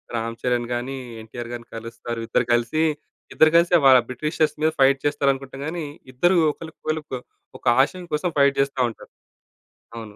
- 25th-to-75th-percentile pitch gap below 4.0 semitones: No, average, 4.5 semitones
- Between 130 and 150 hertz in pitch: Yes, low, 135 Hz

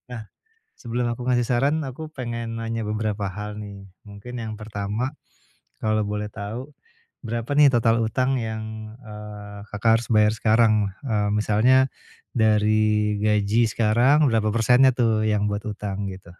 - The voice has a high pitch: No, low, 110 Hz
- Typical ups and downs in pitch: No, narrow, 2.2 semitones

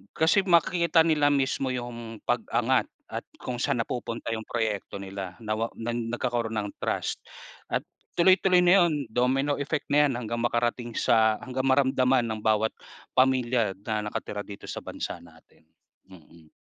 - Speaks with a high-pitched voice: No, low, 120 Hz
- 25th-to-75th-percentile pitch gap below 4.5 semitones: Yes, average, 3.9 semitones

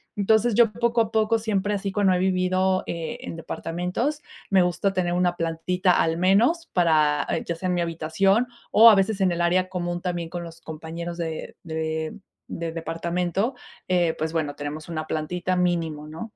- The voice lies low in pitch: No, medium, 180 Hz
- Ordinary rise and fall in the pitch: Yes, average, 3.0 semitones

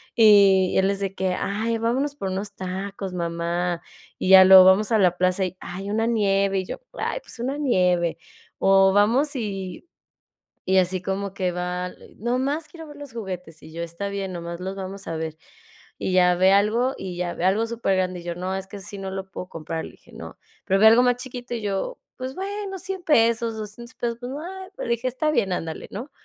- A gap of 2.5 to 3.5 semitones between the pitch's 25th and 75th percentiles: No, average, 4.3 semitones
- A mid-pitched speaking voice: No, high, 195 Hz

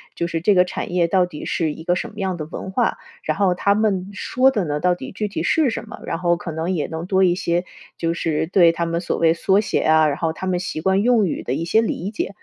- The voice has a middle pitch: Yes, medium, 180 Hz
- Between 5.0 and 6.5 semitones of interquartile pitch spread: No, average, 2.9 semitones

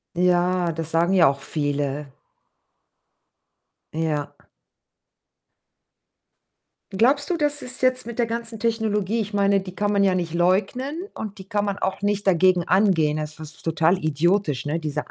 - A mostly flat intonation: No, average, 4.5 semitones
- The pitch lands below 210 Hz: Yes, medium, 185 Hz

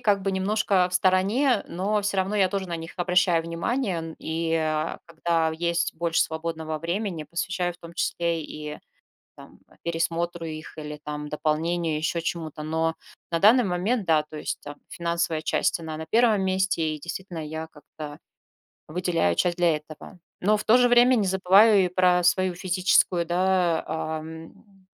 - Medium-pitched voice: Yes, medium, 170 Hz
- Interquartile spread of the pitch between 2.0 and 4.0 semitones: Yes, average, 2.9 semitones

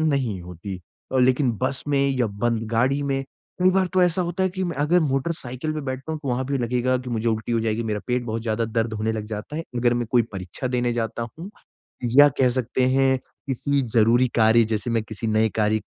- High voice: No, low, 125 Hz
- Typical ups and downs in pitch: Yes, average, 3.7 semitones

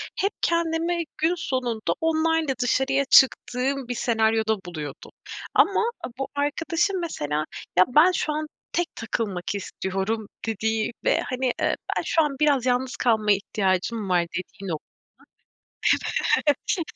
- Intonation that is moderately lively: No, wide, 6.7 semitones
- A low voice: No, very high, 250 Hz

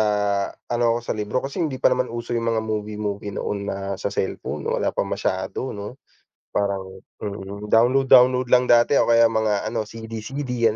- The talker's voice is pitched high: No, low, 110 Hz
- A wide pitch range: No, average, 3.0 semitones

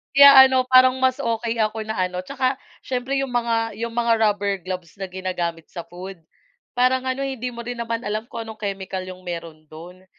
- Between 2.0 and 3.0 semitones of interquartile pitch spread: No, average, 5.3 semitones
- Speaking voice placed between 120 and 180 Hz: No, high, 225 Hz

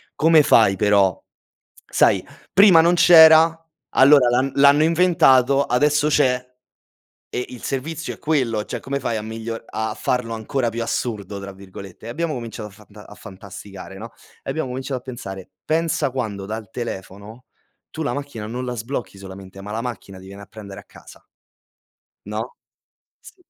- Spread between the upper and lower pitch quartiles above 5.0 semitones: Yes, wide, 5.4 semitones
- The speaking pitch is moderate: No, low, 120 Hz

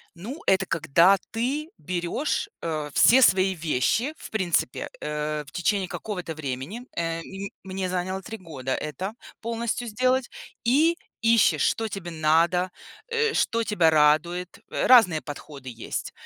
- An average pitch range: No, wide, 6.2 semitones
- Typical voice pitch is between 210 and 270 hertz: No, medium, 185 Hz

